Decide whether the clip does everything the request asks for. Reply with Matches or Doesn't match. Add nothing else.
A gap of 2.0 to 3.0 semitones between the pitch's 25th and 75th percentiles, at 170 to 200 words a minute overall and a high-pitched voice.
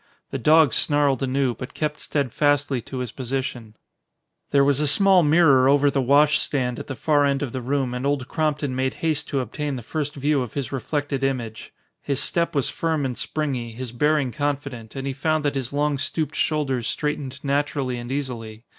Doesn't match